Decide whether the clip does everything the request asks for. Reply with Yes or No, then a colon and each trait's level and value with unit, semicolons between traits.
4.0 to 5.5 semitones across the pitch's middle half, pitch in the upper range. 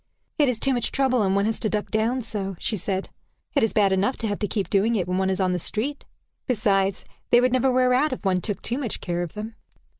Yes: average, 4.4 semitones; high, 215 Hz